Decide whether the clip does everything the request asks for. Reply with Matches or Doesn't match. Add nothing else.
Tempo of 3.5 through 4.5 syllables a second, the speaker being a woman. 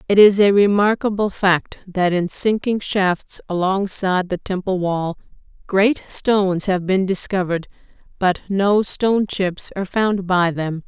Matches